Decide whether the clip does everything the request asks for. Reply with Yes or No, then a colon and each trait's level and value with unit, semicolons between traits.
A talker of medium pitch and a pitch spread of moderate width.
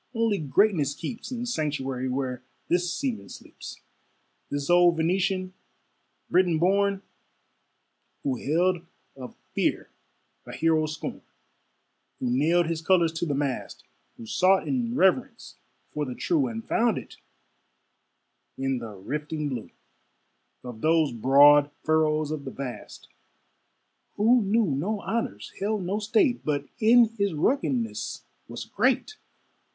No: medium, 165 Hz; wide, 6.2 semitones